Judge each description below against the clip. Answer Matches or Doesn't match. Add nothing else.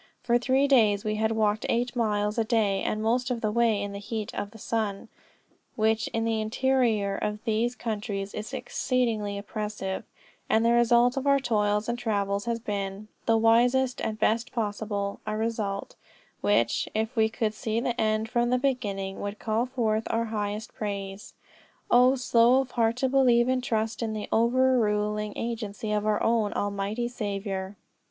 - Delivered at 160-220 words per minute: Matches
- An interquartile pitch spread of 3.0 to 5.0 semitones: Doesn't match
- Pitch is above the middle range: Matches